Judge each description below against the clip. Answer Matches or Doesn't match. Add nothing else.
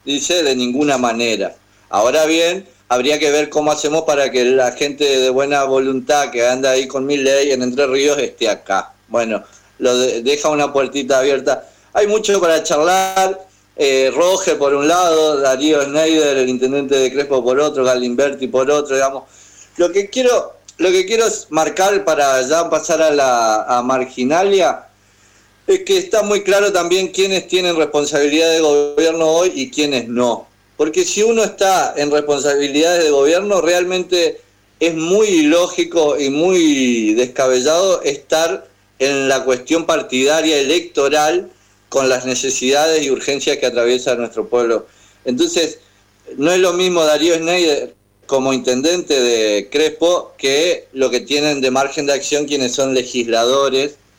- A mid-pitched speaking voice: Matches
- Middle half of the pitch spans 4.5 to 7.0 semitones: Matches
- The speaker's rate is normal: Matches